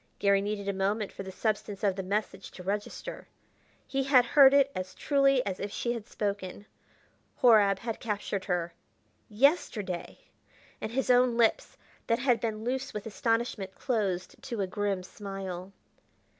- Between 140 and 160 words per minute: Yes, average, 155 wpm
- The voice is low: No, high, 210 Hz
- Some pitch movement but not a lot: Yes, average, 3.6 semitones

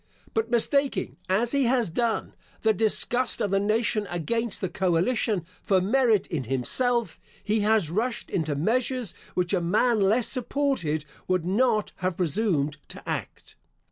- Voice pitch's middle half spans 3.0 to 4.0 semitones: No, average, 4.9 semitones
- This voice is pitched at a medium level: No, high, 215 Hz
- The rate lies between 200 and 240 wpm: No, average, 145 wpm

